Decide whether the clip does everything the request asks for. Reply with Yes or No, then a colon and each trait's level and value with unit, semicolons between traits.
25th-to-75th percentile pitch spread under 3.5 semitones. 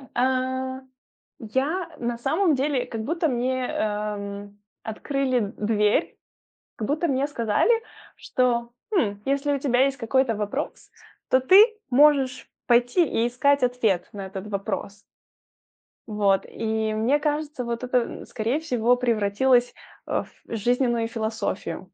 No: average, 3.8 semitones